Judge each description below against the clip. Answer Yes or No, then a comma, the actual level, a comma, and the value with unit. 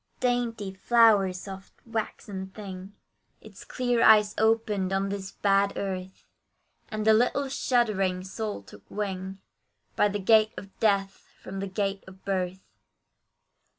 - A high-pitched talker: Yes, high, 200 Hz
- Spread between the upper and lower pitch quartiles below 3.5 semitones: Yes, narrow, 2.4 semitones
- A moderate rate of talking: No, slow, 130 wpm